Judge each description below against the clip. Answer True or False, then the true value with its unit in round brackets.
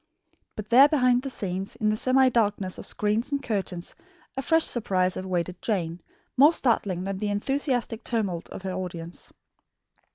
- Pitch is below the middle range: False (210 Hz)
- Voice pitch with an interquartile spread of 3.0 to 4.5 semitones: False (5.3 semitones)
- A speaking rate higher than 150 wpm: True (160 wpm)